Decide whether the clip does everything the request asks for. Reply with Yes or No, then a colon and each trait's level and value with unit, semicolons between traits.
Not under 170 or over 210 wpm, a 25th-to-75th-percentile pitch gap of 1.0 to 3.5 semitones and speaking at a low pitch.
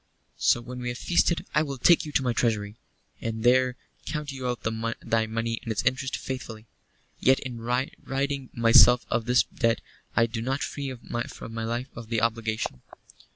Yes: average, 175 wpm; narrow, 2.5 semitones; low, 120 Hz